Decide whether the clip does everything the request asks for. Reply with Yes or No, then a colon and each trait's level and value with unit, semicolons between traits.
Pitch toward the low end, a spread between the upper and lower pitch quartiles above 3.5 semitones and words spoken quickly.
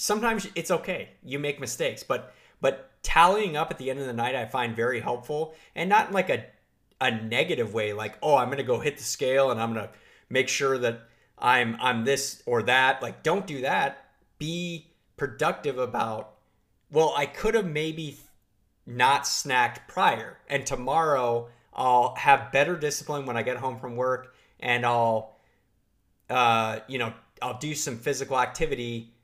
No: low, 130 Hz; average, 4.2 semitones; average, 170 wpm